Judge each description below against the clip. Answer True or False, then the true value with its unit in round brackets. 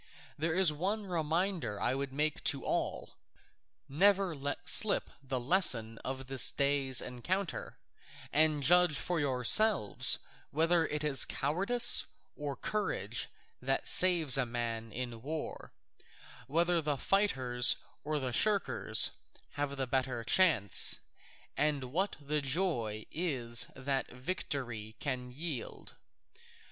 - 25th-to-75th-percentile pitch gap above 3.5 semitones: True (5.3 semitones)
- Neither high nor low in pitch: True (145 Hz)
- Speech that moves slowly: True (120 wpm)